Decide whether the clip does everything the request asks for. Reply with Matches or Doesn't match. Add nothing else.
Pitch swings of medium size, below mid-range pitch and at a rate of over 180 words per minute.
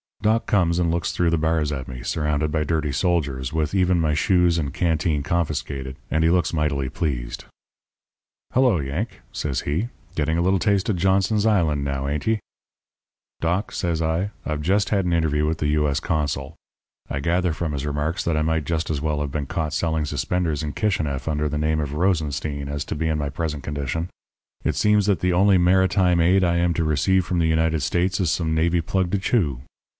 Matches